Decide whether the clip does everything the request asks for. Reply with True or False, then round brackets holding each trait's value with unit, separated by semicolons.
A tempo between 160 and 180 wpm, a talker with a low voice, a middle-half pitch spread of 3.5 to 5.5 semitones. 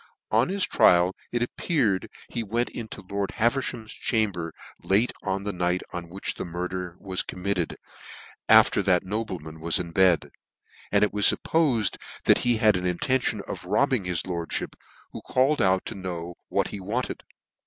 True (165 wpm; 100 Hz; 4.1 semitones)